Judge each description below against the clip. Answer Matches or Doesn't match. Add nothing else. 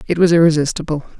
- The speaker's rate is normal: Matches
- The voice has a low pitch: Doesn't match